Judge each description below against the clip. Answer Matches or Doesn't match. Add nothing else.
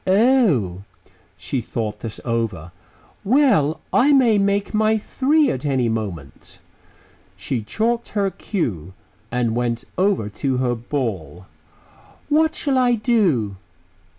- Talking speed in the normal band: Doesn't match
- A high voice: Doesn't match